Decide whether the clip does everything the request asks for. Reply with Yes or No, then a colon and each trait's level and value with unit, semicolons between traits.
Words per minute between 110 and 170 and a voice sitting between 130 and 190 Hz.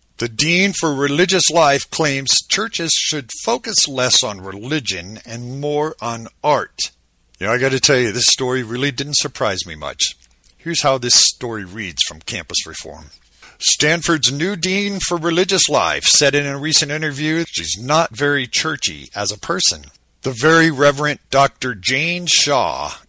Yes: average, 165 wpm; medium, 140 Hz